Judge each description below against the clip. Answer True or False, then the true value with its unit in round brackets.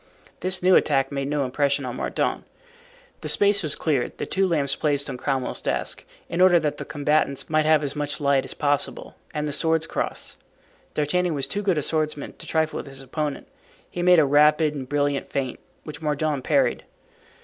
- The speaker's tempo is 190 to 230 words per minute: True (195 wpm)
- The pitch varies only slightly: True (2.1 semitones)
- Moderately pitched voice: True (150 Hz)